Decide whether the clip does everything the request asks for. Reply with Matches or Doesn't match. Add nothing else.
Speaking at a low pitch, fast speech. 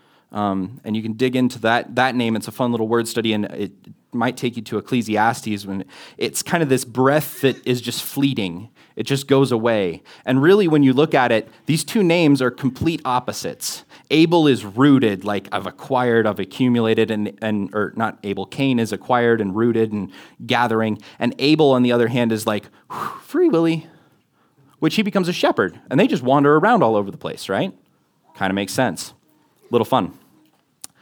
Doesn't match